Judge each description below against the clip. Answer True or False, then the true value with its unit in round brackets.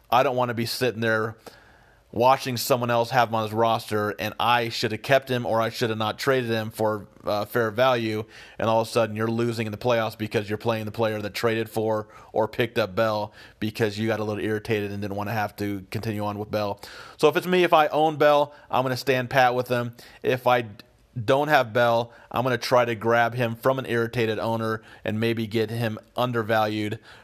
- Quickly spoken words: True (235 wpm)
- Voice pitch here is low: True (115 Hz)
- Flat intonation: True (2.0 semitones)